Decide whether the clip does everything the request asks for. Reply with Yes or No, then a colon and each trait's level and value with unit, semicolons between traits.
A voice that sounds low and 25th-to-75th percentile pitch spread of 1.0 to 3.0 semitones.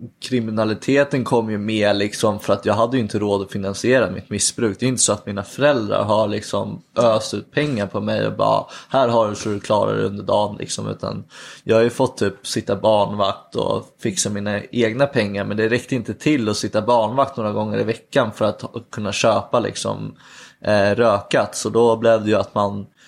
Yes: low, 110 Hz; average, 2.7 semitones